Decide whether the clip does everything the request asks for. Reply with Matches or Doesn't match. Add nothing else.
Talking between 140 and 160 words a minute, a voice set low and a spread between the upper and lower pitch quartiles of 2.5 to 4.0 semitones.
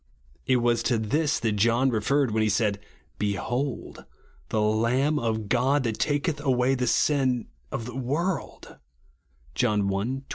Matches